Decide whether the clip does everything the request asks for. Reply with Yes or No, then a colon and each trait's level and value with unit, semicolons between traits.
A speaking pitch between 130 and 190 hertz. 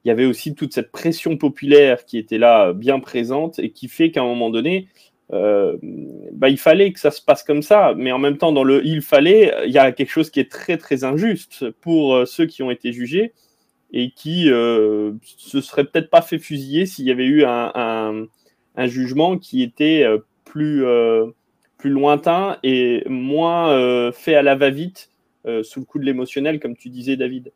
Yes: medium, 140 Hz